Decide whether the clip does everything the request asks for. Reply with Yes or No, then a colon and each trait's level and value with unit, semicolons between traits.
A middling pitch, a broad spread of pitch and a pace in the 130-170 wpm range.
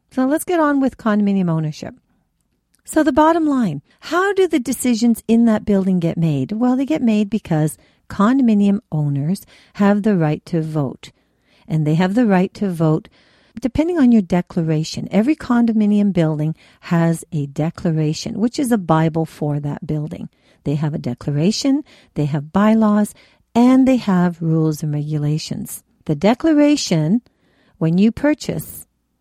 No: high, 200 Hz; wide, 7.2 semitones; average, 150 wpm